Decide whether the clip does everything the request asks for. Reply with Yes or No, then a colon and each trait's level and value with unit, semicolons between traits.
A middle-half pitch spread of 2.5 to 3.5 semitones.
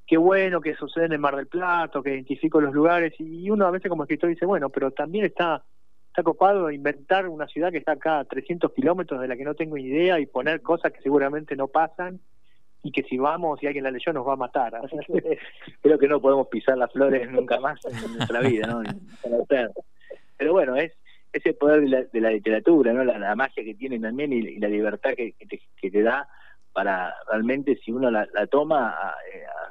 No: average, 4.3 semitones